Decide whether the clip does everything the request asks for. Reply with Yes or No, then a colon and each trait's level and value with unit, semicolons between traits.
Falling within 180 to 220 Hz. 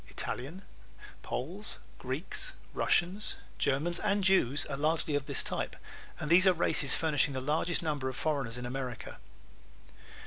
No: medium, 150 Hz